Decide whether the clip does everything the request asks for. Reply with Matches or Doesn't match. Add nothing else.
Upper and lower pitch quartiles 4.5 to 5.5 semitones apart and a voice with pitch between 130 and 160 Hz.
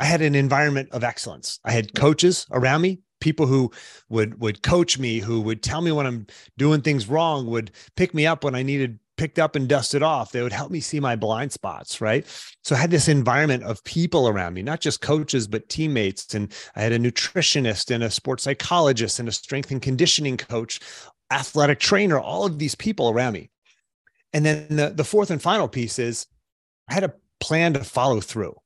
Matches